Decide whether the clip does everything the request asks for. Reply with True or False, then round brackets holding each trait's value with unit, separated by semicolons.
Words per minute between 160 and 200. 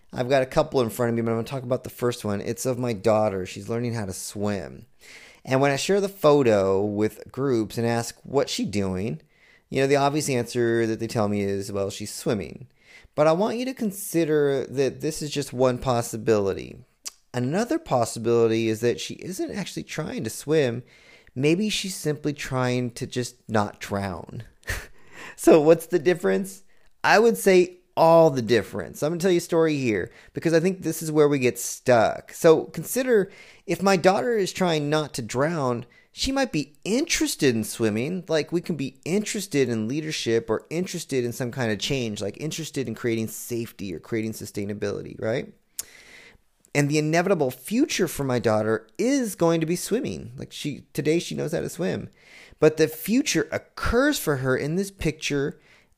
True (190 wpm)